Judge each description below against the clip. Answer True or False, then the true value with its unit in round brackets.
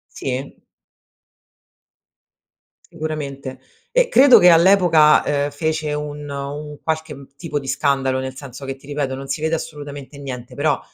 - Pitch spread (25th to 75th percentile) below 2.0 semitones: False (2.4 semitones)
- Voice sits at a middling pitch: True (145 Hz)